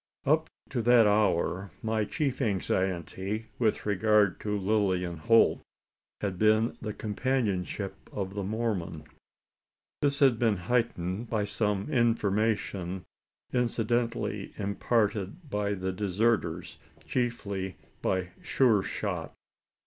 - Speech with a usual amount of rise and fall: Yes, average, 3.2 semitones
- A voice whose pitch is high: No, low, 105 Hz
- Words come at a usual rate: No, slow, 105 wpm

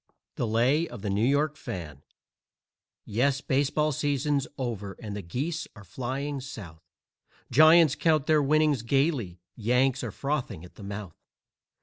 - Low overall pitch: Yes, low, 130 Hz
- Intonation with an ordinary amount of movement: No, wide, 5.7 semitones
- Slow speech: No, average, 145 wpm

